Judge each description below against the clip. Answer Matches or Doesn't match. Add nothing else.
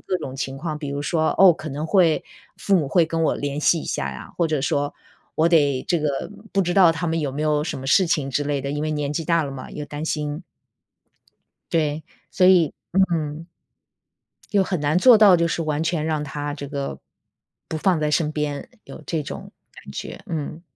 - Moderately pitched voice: Matches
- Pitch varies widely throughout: Doesn't match